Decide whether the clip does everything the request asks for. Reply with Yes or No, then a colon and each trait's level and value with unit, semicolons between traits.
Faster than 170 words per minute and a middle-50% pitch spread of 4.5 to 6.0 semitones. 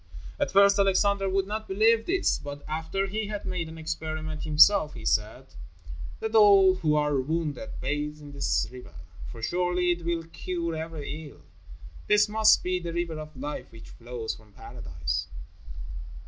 No: average, 160 wpm; average, 4.8 semitones